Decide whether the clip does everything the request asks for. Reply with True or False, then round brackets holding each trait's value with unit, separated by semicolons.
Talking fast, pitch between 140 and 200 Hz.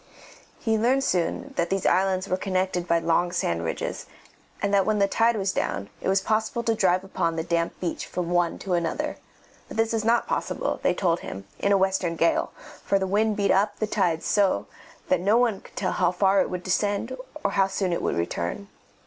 True (215 wpm; 190 Hz)